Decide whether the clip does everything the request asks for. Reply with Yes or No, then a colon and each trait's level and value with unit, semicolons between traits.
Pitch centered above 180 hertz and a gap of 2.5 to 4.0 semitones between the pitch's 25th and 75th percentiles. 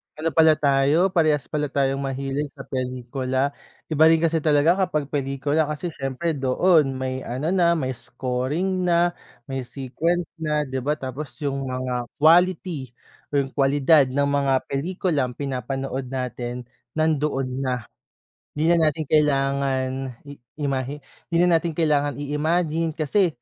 No: medium, 145 Hz; average, 3.1 semitones